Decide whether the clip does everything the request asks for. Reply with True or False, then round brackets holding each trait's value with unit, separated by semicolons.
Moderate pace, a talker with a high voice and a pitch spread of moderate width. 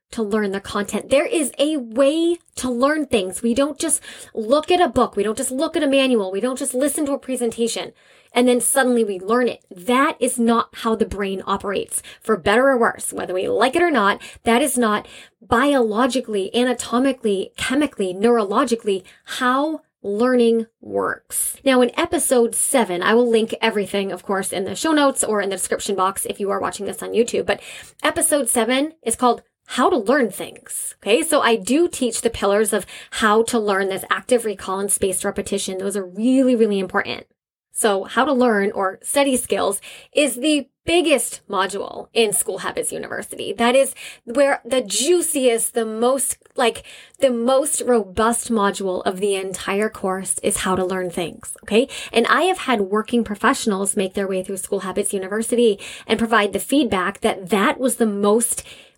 True (185 wpm; 230 Hz; 4.8 semitones)